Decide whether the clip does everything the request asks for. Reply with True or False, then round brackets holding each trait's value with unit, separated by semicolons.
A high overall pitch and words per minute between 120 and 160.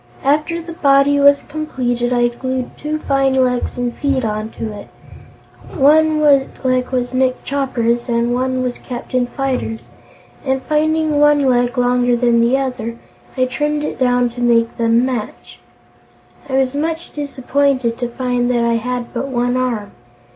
True (255 Hz; 155 wpm)